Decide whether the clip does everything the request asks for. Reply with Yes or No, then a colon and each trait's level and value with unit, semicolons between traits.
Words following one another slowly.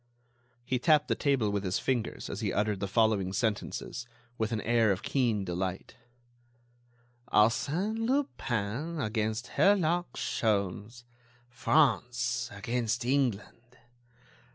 Yes: slow, 110 wpm